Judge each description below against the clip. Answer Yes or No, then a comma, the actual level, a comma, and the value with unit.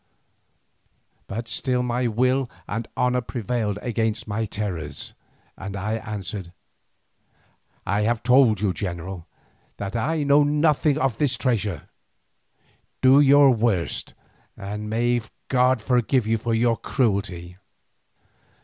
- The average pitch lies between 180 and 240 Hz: No, low, 115 Hz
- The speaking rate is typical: No, slow, 120 wpm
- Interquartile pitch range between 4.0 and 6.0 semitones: No, average, 3.6 semitones